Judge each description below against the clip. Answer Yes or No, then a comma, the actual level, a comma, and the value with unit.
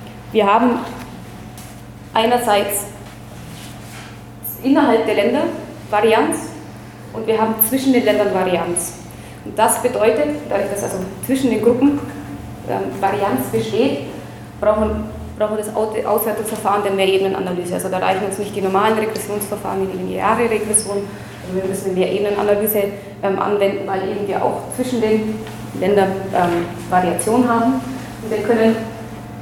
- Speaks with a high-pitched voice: Yes, high, 205 Hz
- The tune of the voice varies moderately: Yes, average, 3.0 semitones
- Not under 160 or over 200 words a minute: No, average, 130 wpm